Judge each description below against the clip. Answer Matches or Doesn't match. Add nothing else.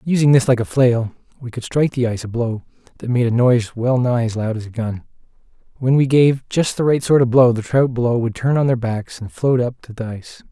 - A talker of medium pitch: Doesn't match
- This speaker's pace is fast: Matches